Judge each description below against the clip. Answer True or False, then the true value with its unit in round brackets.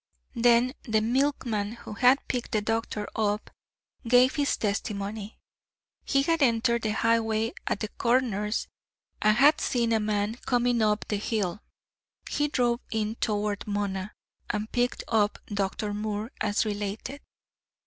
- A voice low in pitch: False (220 Hz)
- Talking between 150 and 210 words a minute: False (140 wpm)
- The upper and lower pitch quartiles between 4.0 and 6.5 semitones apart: False (2.6 semitones)